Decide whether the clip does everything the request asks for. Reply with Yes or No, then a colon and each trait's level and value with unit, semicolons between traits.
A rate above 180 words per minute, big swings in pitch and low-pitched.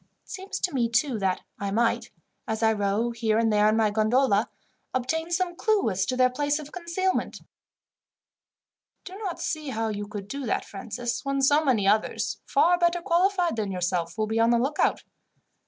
No: average, 190 wpm; wide, 6.8 semitones; high, 240 Hz